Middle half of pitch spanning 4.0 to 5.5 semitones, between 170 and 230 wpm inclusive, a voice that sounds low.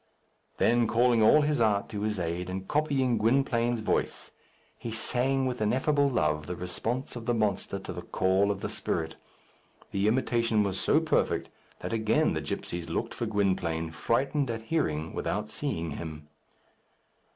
No: average, 4.8 semitones; average, 160 wpm; low, 110 Hz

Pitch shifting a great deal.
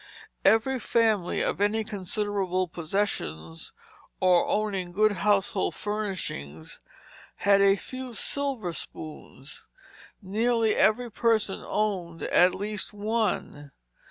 No: average, 3.3 semitones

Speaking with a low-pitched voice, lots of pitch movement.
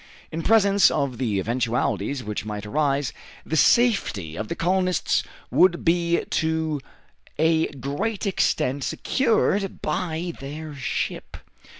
No: medium, 155 Hz; wide, 5.8 semitones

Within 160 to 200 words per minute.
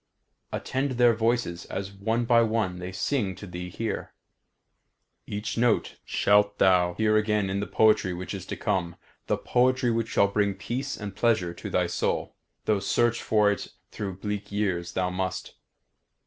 Yes: average, 165 wpm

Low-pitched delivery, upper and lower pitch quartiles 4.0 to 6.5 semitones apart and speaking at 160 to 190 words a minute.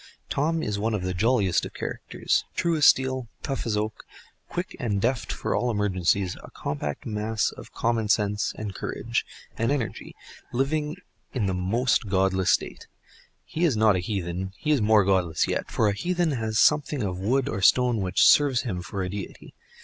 Yes: low, 110 Hz; average, 5.2 semitones; average, 180 wpm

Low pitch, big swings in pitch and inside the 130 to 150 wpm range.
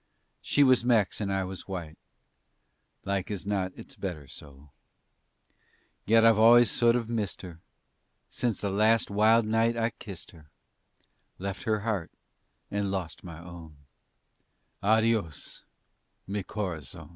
No: low, 100 Hz; average, 4.0 semitones; slow, 135 wpm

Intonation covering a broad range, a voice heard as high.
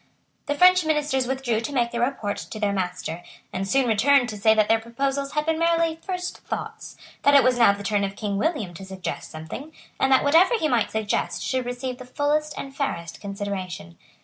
Yes: wide, 6.1 semitones; high, 245 Hz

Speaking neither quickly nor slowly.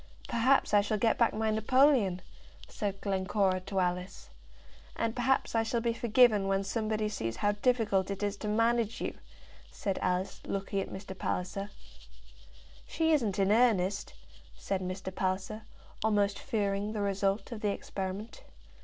Yes: average, 150 wpm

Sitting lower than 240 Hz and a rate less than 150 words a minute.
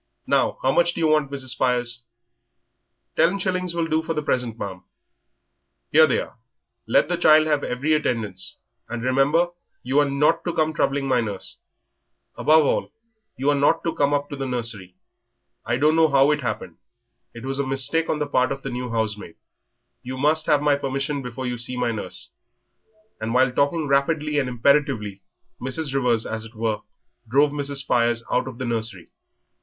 No: low, 135 Hz; average, 185 wpm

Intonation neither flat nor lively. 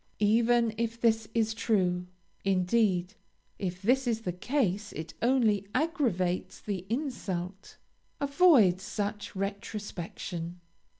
Yes: average, 4.1 semitones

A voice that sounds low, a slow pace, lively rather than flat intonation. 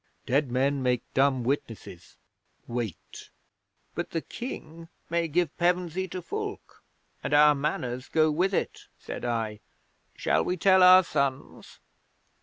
No: medium, 150 Hz; slow, 130 wpm; wide, 5.8 semitones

